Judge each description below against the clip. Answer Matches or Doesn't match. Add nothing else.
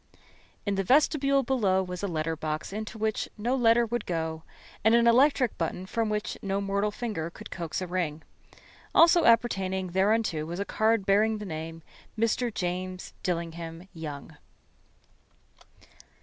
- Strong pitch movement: Doesn't match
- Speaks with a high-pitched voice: Matches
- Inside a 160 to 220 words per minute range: Doesn't match